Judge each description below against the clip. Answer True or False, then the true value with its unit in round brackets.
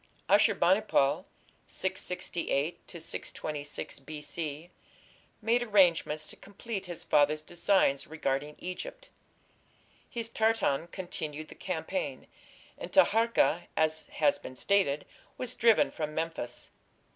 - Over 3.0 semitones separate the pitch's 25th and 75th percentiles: True (5.1 semitones)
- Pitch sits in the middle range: True (170 Hz)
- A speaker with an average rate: False (105 wpm)